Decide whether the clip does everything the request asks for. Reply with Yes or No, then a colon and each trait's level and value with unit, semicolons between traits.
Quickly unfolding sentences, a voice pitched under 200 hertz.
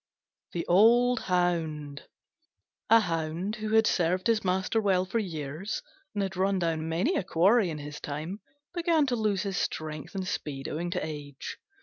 No: average, 165 wpm; medium, 185 Hz